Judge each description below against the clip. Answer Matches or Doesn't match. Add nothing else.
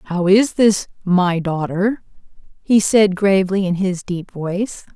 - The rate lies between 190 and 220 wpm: Doesn't match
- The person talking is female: Matches